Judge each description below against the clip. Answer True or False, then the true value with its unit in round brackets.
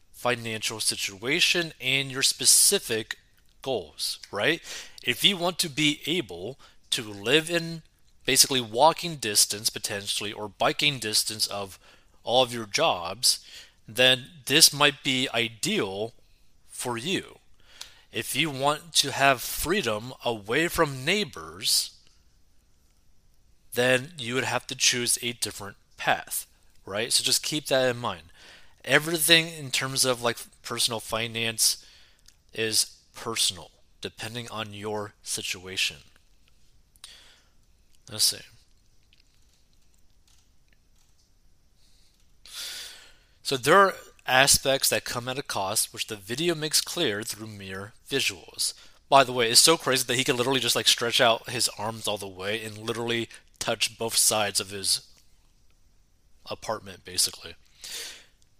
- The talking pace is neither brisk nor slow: False (125 wpm)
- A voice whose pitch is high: False (115 Hz)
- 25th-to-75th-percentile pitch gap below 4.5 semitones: False (5.0 semitones)